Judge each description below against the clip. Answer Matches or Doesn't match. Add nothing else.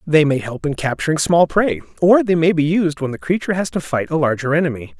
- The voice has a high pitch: Doesn't match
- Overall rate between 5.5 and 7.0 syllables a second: Matches